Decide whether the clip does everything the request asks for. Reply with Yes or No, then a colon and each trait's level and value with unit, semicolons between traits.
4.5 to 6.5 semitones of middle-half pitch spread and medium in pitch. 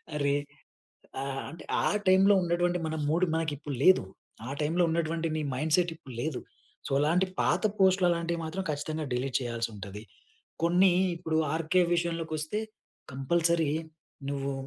No: average, 3.0 semitones; medium, 160 Hz